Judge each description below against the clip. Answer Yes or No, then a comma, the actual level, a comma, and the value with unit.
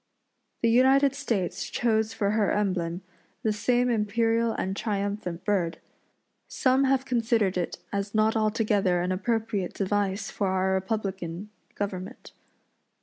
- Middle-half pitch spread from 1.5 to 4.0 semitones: Yes, average, 3.1 semitones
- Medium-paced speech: No, slow, 125 wpm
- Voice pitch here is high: Yes, high, 210 Hz